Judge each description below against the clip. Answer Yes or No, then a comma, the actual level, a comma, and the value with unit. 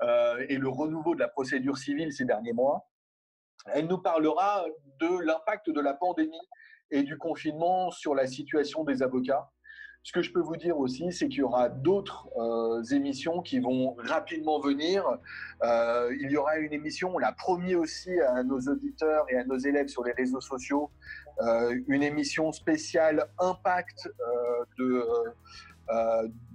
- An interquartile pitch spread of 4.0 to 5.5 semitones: Yes, average, 5.2 semitones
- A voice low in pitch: No, medium, 150 Hz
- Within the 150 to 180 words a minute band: Yes, average, 170 wpm